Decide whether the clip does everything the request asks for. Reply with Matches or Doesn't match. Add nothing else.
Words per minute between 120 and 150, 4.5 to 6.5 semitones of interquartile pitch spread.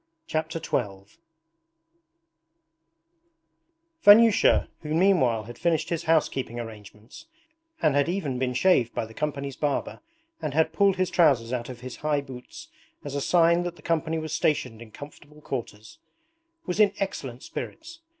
Matches